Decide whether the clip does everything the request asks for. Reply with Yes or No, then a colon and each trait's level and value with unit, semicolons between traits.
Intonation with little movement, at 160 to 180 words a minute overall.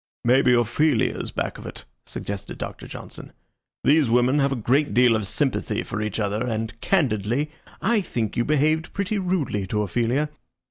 No: wide, 5.4 semitones; average, 170 wpm